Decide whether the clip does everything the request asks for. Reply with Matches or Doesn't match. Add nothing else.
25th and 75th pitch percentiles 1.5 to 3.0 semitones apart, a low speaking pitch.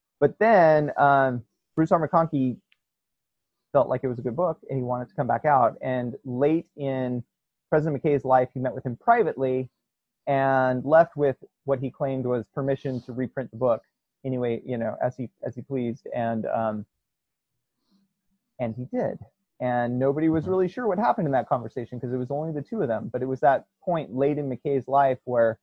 Matches